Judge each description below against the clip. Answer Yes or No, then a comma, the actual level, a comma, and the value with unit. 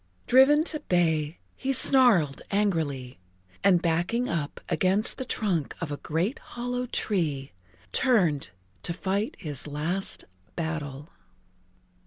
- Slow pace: Yes, slow, 115 wpm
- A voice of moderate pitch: Yes, medium, 175 Hz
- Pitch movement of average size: No, wide, 6.9 semitones